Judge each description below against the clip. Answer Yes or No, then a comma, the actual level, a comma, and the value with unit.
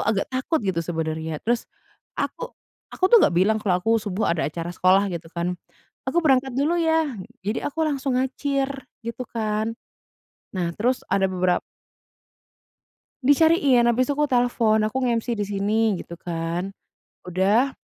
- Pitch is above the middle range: Yes, high, 220 Hz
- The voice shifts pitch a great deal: Yes, wide, 6.2 semitones